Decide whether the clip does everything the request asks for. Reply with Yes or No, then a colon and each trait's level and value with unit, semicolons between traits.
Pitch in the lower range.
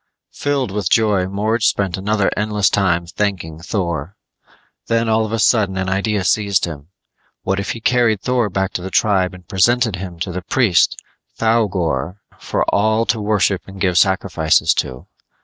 Yes: low, 100 Hz